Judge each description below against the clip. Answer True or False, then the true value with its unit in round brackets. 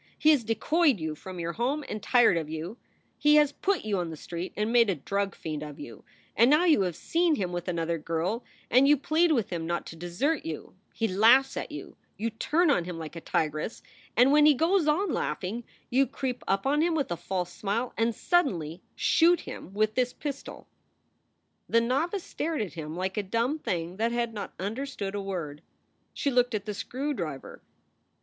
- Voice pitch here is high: True (220 Hz)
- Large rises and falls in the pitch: True (8.0 semitones)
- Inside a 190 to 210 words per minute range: True (205 wpm)